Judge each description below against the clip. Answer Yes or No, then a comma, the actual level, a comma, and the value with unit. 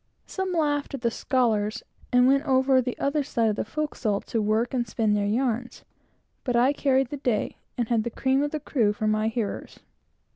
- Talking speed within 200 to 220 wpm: Yes, fast, 205 wpm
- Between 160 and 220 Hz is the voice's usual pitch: No, high, 245 Hz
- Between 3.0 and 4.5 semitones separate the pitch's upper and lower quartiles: Yes, average, 3.8 semitones